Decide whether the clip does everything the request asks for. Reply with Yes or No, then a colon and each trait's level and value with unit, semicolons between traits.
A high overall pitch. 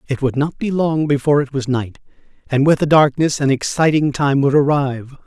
No: medium, 140 Hz